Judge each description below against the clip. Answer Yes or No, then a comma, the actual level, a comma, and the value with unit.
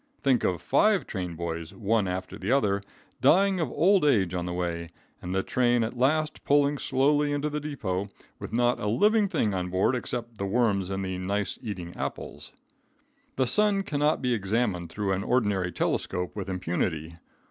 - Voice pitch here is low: Yes, low, 105 Hz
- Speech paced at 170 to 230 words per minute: Yes, average, 180 wpm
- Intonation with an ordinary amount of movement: No, wide, 7.4 semitones